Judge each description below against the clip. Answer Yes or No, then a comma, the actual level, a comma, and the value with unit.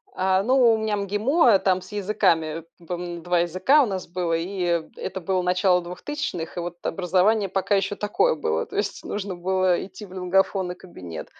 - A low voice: No, medium, 185 Hz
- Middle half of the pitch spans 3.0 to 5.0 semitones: No, narrow, 2.6 semitones